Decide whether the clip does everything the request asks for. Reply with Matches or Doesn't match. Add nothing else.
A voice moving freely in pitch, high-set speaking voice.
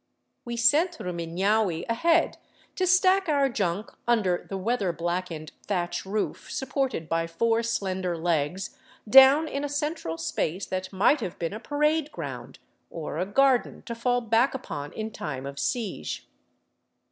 Matches